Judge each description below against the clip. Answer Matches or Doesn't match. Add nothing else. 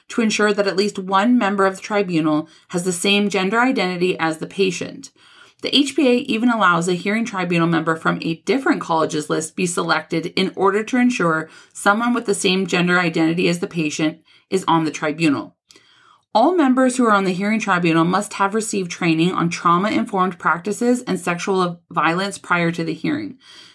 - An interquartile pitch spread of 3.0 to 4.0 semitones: Matches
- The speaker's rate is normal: Matches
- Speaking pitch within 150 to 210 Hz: Matches